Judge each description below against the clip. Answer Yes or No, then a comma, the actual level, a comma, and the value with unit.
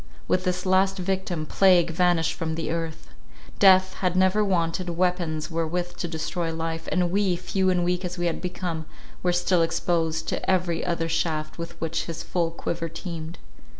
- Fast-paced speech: No, average, 175 wpm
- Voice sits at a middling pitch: Yes, medium, 175 Hz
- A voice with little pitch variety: Yes, narrow, 1.9 semitones